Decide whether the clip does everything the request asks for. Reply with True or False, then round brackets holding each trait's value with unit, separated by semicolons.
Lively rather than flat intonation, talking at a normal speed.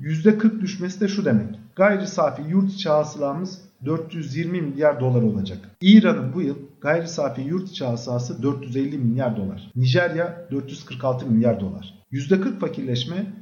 True (6.5 semitones; 130 wpm)